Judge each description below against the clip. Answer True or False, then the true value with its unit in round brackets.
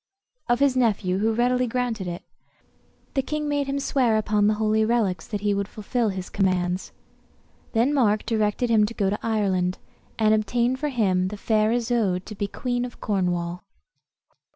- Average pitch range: True (3.6 semitones)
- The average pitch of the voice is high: True (215 Hz)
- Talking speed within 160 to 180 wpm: True (175 wpm)